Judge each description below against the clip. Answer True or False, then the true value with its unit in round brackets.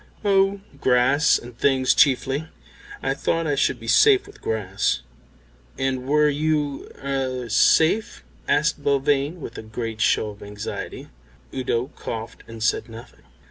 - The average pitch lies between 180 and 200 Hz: False (135 Hz)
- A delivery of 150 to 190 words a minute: False (140 wpm)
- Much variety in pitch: False (4.6 semitones)